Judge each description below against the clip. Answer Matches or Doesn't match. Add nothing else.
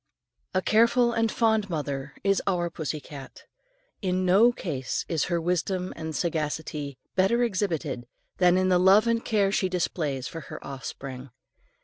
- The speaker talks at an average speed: Matches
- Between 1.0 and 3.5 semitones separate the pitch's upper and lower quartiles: Doesn't match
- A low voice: Doesn't match